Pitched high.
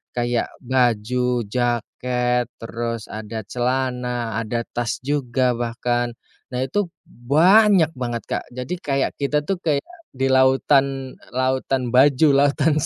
No: low, 125 Hz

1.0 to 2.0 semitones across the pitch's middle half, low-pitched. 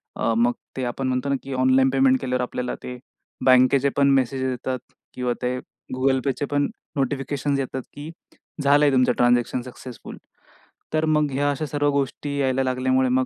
Yes: narrow, 1.7 semitones; low, 130 Hz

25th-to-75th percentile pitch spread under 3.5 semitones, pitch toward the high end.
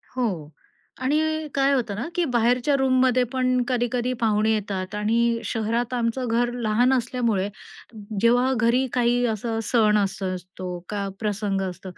Yes: average, 3.1 semitones; high, 235 Hz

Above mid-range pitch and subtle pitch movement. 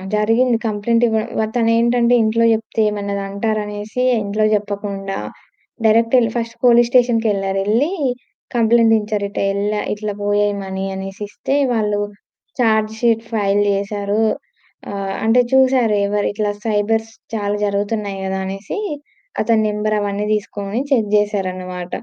Yes: high, 210 Hz; narrow, 2.0 semitones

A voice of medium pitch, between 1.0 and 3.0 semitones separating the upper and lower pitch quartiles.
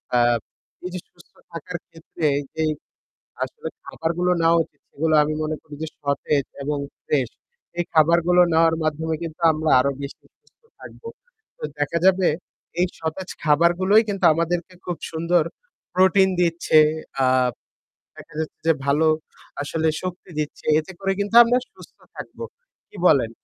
Yes: medium, 165 Hz; narrow, 2.5 semitones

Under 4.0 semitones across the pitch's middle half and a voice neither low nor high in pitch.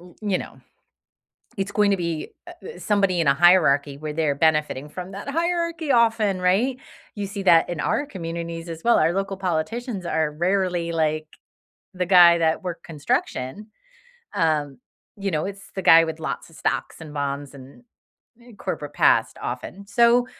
No: average, 4.3 semitones; medium, 175 Hz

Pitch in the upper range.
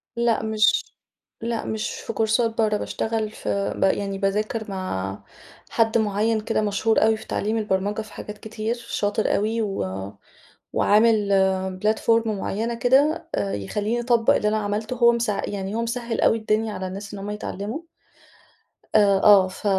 Yes: high, 215 Hz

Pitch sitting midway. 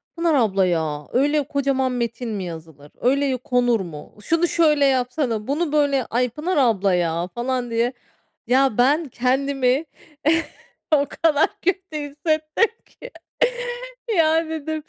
No: very high, 265 Hz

